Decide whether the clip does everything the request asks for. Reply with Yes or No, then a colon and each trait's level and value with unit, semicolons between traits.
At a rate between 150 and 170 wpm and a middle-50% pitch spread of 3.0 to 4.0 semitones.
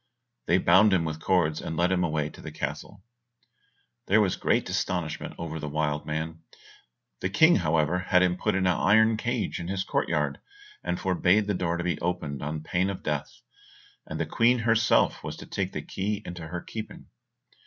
No: average, 195 wpm; average, 3.6 semitones